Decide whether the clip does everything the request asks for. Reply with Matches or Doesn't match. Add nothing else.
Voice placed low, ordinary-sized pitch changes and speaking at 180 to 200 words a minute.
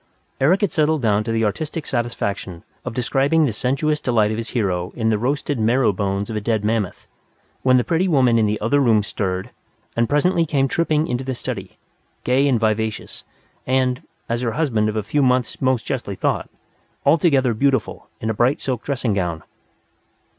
Matches